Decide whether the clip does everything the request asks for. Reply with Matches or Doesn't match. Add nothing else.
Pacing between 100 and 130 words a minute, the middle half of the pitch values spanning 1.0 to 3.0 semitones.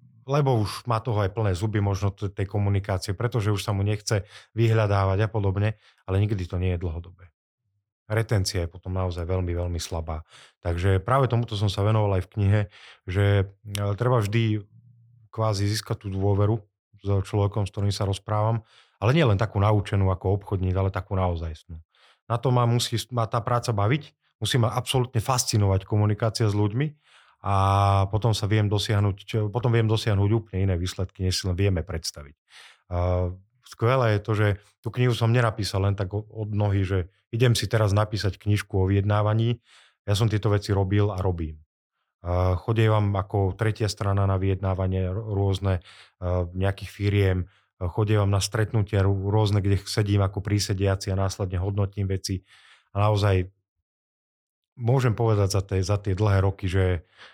Doesn't match